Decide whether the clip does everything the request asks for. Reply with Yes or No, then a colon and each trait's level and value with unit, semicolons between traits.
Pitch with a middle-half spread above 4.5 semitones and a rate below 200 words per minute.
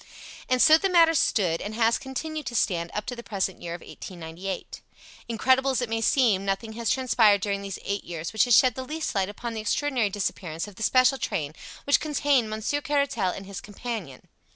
No: average, 5.1 semitones; fast, 205 wpm